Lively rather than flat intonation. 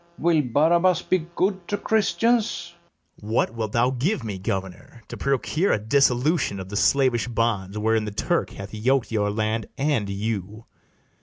Yes: wide, 6.6 semitones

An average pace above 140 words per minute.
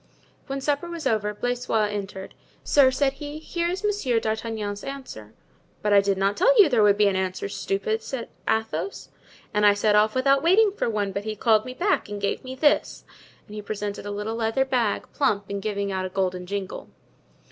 Yes: average, 200 wpm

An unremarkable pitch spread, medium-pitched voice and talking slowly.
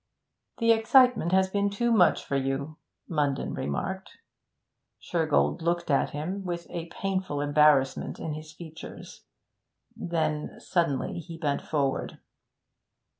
Yes: average, 4.3 semitones; medium, 165 Hz; slow, 120 wpm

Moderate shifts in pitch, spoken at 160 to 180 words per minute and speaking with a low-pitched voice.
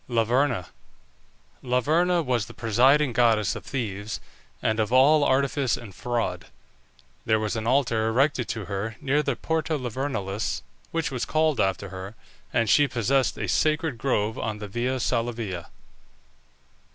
No: average, 4.2 semitones; average, 140 wpm; low, 120 Hz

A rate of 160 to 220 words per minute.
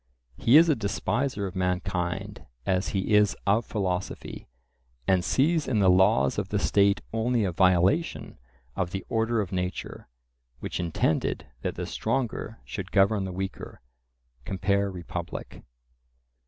No: average, 140 wpm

